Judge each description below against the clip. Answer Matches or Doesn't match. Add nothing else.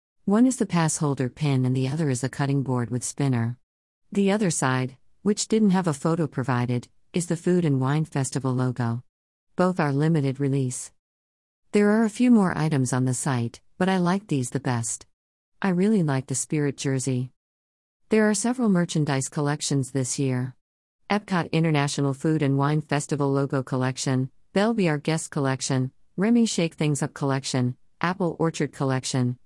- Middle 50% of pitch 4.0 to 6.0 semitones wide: Matches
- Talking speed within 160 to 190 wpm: Matches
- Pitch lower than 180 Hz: Matches